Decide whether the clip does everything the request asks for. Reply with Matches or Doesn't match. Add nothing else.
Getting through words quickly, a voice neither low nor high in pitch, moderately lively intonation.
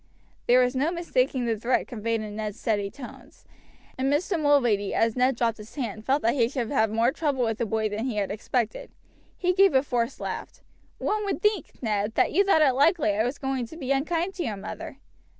Doesn't match